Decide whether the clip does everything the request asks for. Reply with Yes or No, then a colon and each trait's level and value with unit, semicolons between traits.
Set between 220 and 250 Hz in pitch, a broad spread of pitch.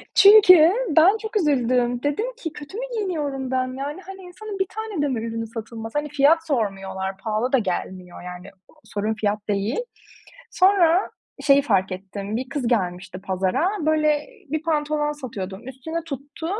No: very high, 270 Hz; wide, 7.1 semitones